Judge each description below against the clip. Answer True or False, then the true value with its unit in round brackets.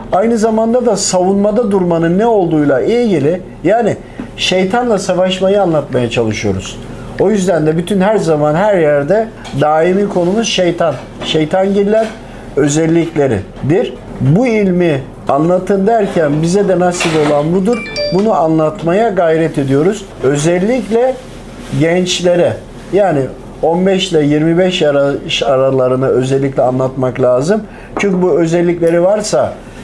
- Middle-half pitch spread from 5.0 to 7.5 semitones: True (5.5 semitones)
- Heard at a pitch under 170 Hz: False (175 Hz)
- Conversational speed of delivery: True (110 wpm)